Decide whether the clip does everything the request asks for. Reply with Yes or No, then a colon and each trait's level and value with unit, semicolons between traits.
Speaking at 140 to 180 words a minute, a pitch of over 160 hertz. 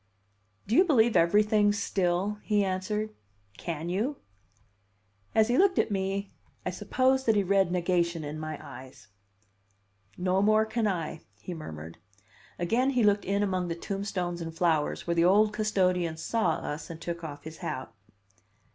Yes: average, 155 wpm; high, 190 Hz